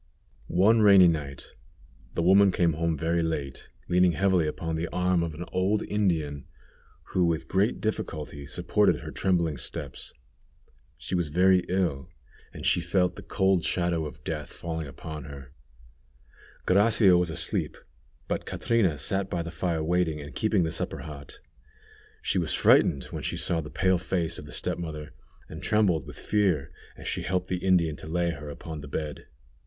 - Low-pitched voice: Yes, very low, 85 Hz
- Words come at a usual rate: Yes, average, 170 wpm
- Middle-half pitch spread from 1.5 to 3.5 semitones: Yes, average, 3.1 semitones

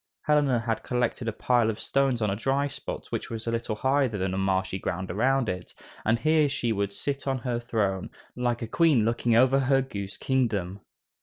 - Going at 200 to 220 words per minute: Yes, fast, 205 wpm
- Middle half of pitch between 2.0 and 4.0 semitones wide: No, average, 4.5 semitones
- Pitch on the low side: Yes, low, 120 Hz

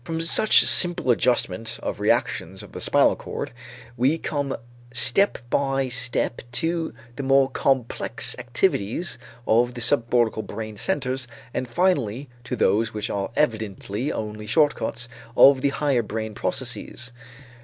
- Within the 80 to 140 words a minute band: Yes, slow, 135 wpm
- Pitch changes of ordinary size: Yes, average, 3.9 semitones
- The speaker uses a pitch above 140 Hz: No, low, 125 Hz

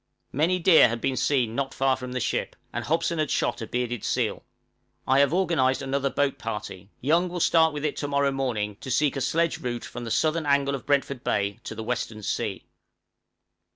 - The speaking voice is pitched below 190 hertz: Yes, low, 135 Hz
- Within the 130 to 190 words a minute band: No, fast, 205 wpm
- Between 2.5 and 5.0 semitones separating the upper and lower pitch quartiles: Yes, average, 3.7 semitones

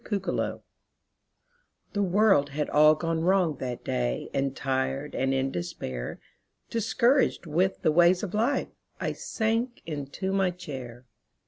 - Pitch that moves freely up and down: Yes, wide, 6.4 semitones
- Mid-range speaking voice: Yes, medium, 160 Hz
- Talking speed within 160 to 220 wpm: No, slow, 135 wpm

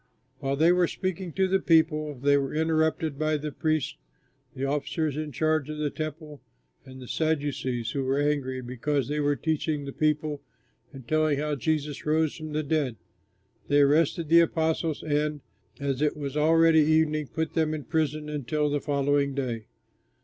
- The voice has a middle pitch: Yes, medium, 150 Hz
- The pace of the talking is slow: No, average, 170 wpm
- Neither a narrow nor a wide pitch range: No, narrow, 1.9 semitones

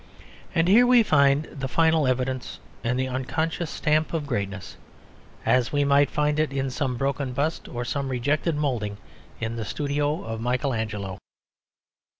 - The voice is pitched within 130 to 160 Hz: Yes, medium, 140 Hz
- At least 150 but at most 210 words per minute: Yes, average, 155 wpm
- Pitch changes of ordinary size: Yes, average, 3.4 semitones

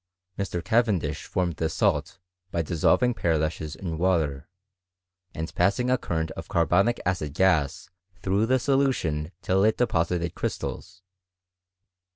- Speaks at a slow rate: Yes, slow, 125 wpm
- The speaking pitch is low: Yes, very low, 90 Hz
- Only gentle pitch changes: No, average, 4.0 semitones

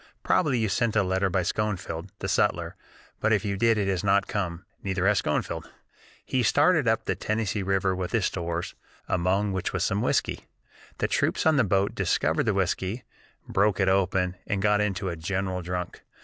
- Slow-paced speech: No, average, 190 wpm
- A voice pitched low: Yes, very low, 95 Hz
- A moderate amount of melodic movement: No, narrow, 2.3 semitones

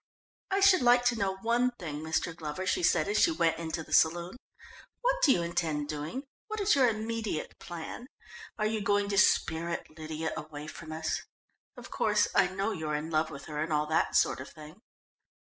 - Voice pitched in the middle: Yes, medium, 170 Hz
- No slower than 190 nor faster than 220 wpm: Yes, average, 200 wpm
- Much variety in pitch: Yes, wide, 6.2 semitones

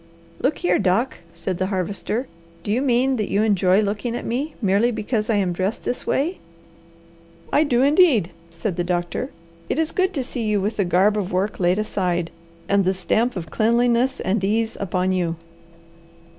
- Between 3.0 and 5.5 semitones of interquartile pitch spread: Yes, average, 4.6 semitones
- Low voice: No, high, 210 Hz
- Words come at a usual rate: Yes, average, 185 wpm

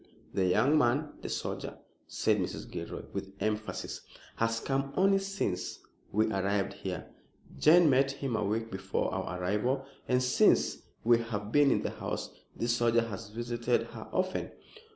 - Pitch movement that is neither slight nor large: Yes, average, 4.8 semitones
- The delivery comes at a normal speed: Yes, average, 155 wpm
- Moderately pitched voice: No, low, 115 Hz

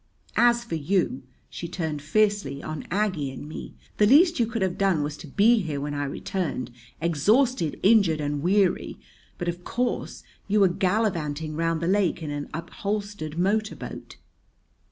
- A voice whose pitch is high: No, medium, 175 Hz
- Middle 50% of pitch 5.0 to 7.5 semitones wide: Yes, average, 5.3 semitones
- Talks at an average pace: Yes, average, 165 wpm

